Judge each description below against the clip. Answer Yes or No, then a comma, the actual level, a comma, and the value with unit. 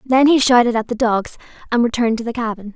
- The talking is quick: Yes, fast, 240 wpm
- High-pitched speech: Yes, high, 235 Hz